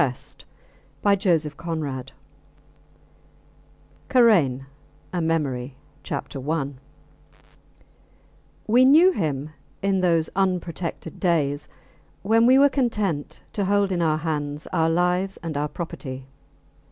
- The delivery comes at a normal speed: No, slow, 105 wpm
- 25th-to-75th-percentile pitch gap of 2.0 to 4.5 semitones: No, average, 5.0 semitones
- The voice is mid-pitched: Yes, medium, 165 Hz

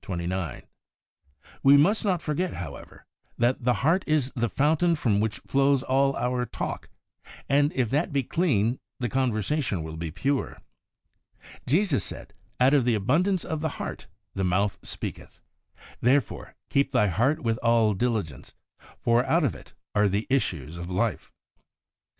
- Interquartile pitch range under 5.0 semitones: No, wide, 5.6 semitones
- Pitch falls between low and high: No, low, 125 Hz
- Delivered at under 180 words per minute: Yes, average, 155 wpm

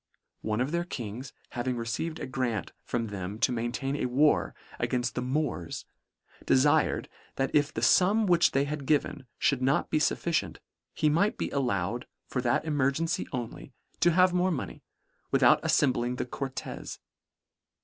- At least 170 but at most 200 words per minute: No, average, 155 wpm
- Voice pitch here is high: No, low, 135 Hz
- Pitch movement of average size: Yes, average, 4.1 semitones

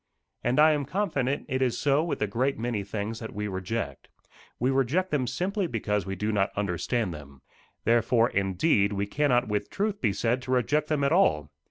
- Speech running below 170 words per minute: No, average, 195 wpm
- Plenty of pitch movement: Yes, wide, 5.7 semitones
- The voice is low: Yes, low, 120 Hz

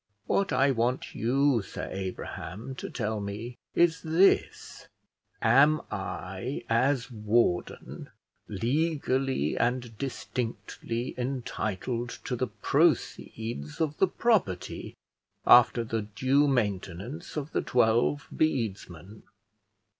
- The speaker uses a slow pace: Yes, slow, 100 wpm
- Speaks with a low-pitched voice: Yes, low, 120 Hz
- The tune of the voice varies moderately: Yes, average, 4.4 semitones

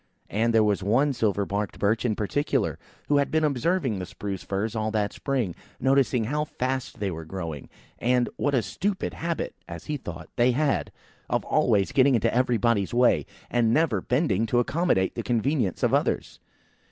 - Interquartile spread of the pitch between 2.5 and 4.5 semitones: No, average, 5.2 semitones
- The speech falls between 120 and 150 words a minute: No, average, 175 wpm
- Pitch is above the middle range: No, low, 120 Hz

